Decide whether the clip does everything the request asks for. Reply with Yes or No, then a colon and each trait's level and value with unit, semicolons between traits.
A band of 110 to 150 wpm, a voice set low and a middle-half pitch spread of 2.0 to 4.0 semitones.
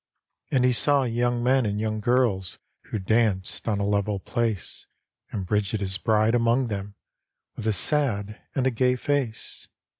No: average, 160 wpm; low, 110 Hz; average, 3.4 semitones